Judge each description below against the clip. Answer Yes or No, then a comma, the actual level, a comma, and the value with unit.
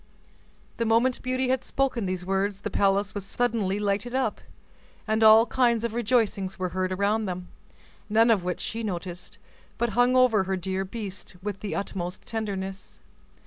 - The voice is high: Yes, high, 205 Hz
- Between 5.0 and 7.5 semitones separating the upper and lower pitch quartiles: No, average, 3.4 semitones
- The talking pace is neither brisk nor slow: Yes, average, 165 wpm